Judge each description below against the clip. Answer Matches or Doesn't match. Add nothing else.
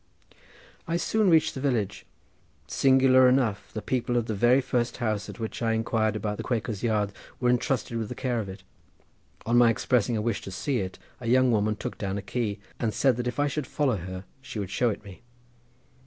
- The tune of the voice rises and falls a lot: Doesn't match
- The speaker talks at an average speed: Doesn't match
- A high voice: Doesn't match